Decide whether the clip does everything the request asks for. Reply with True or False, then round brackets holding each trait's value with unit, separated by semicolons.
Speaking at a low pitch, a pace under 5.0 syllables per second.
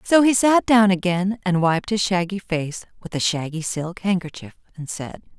False (185 Hz; 4.6 syllables/s)